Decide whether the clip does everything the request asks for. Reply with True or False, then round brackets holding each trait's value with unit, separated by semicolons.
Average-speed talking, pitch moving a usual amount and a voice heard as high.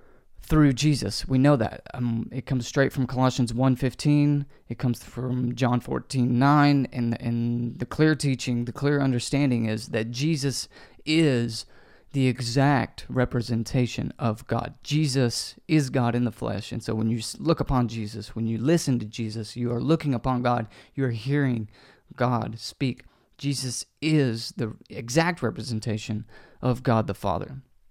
False (155 wpm; 3.3 semitones; 125 Hz)